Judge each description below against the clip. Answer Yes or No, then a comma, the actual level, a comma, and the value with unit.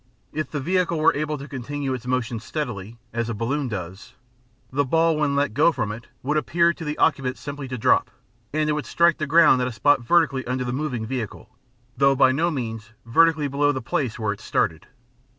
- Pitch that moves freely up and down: No, average, 4.2 semitones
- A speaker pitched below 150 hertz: Yes, low, 135 Hz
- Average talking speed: No, fast, 210 wpm